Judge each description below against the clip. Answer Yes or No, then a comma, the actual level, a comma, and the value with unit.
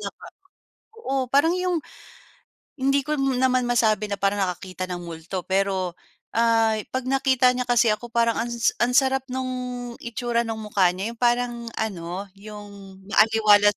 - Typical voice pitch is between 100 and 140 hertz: No, high, 230 Hz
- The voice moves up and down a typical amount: Yes, average, 3.8 semitones